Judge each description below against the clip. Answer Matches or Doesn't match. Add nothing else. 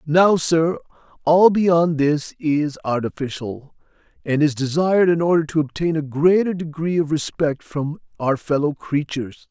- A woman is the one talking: Doesn't match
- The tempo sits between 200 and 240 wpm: Doesn't match